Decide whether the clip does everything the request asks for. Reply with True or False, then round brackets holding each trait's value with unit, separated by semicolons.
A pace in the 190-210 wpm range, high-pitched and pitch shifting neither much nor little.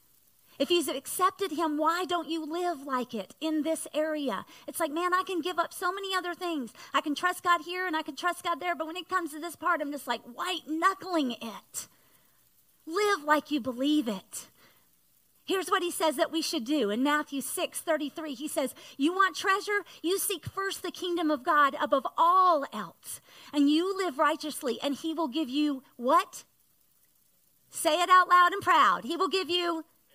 True (200 wpm; 325 Hz; 3.4 semitones)